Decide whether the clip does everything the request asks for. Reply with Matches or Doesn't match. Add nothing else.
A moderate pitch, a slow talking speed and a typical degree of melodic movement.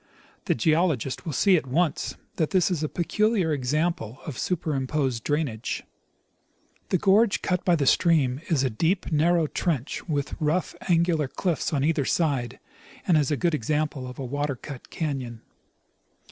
Doesn't match